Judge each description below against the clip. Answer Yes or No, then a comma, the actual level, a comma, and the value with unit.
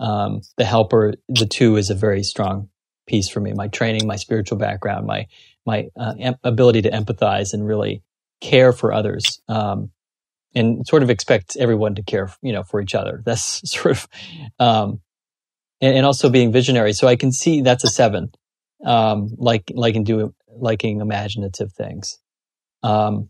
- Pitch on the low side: Yes, low, 110 Hz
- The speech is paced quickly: No, average, 175 wpm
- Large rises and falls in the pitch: No, average, 2.7 semitones